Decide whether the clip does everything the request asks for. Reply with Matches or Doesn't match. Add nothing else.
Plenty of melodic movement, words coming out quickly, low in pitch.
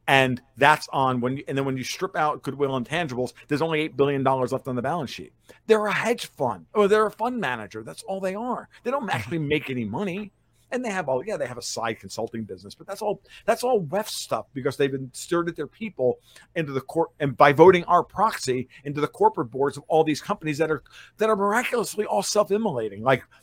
Doesn't match